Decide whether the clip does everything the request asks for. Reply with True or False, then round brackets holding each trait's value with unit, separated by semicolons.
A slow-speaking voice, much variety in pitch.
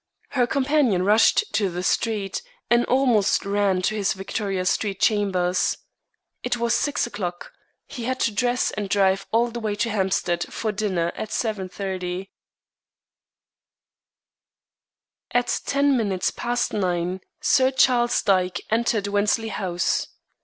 False (130 wpm; 4.0 semitones)